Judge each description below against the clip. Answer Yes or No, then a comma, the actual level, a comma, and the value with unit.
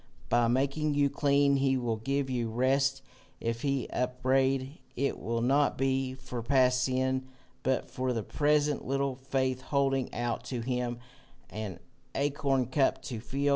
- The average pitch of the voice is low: Yes, low, 130 Hz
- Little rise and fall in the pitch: Yes, narrow, 1.7 semitones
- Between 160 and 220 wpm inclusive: No, average, 150 wpm